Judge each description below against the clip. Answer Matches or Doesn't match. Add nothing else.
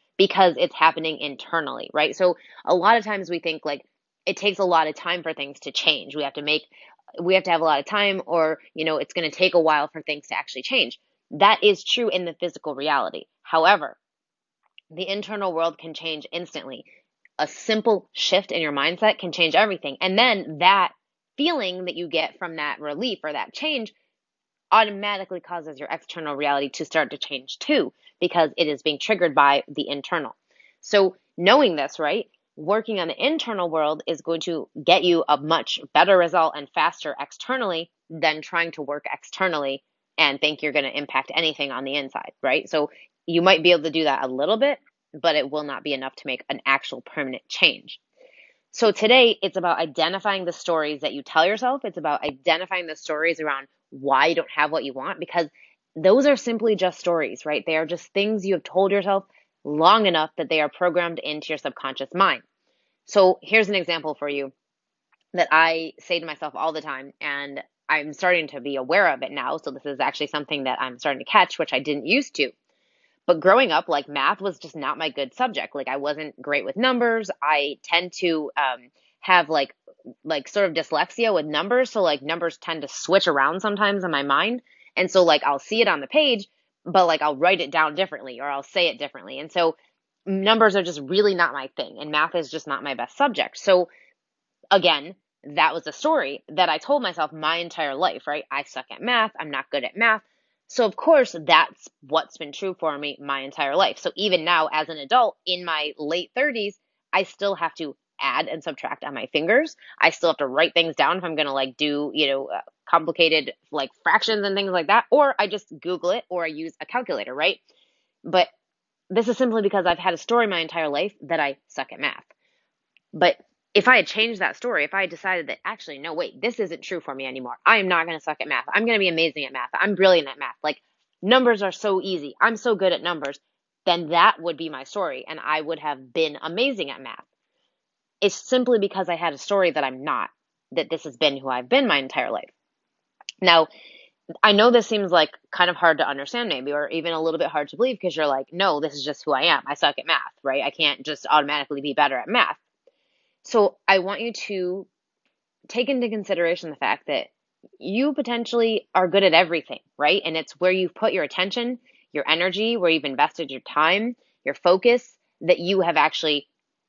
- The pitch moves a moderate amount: Matches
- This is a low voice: Doesn't match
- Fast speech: Matches